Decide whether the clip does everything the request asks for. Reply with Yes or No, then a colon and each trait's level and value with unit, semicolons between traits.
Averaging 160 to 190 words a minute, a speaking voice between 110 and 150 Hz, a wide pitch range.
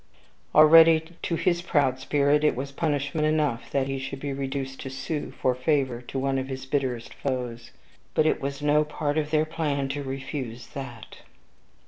No: average, 175 wpm; medium, 140 Hz; narrow, 2.4 semitones